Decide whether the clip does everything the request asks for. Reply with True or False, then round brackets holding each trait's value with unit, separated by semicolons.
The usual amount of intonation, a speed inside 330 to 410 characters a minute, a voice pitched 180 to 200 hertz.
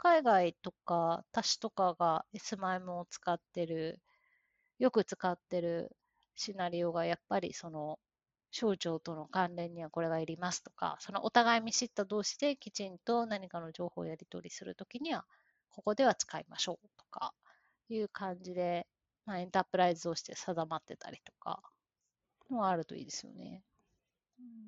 False (4.7 semitones; 320 characters per minute; 185 Hz)